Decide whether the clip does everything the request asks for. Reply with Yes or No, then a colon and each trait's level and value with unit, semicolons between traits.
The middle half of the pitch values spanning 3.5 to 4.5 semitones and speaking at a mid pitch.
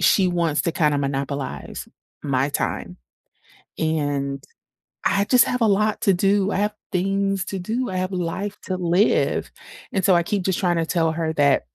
Yes: average, 3.9 semitones; medium, 180 Hz